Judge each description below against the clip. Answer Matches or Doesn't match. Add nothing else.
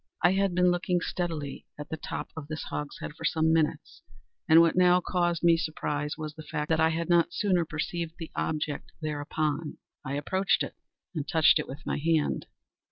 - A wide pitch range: Doesn't match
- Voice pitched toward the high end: Doesn't match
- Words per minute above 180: Matches